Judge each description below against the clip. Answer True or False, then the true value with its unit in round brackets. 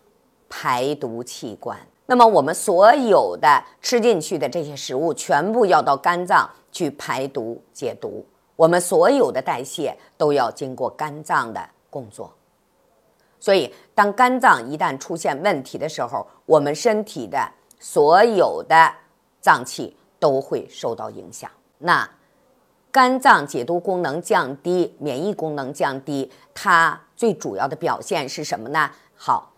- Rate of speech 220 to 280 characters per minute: False (210 characters per minute)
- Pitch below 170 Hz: False (175 Hz)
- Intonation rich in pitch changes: True (7.1 semitones)